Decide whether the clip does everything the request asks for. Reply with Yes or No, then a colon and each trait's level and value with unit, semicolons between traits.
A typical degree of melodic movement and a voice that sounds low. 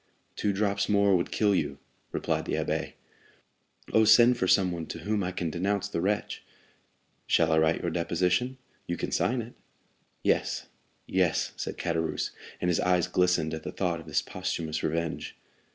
Yes: average, 3.4 semitones; very low, 90 Hz